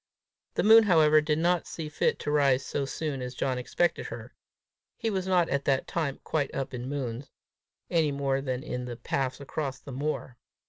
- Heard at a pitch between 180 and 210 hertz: No, medium, 140 Hz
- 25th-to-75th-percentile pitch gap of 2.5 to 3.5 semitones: Yes, average, 3.2 semitones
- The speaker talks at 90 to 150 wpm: No, average, 190 wpm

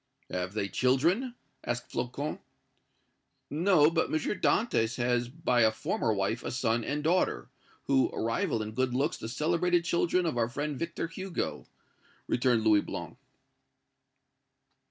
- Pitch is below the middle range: Yes, low, 130 Hz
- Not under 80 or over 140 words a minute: Yes, slow, 135 wpm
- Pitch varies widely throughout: Yes, wide, 6.4 semitones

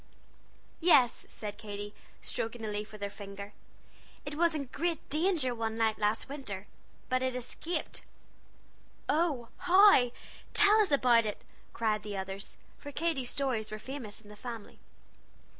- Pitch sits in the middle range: No, high, 240 Hz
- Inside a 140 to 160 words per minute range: Yes, average, 145 wpm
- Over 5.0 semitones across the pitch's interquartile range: Yes, wide, 5.5 semitones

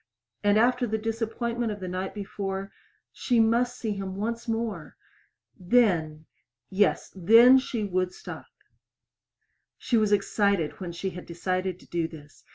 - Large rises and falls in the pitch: No, average, 3.8 semitones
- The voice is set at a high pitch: Yes, high, 205 Hz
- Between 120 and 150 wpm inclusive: Yes, average, 145 wpm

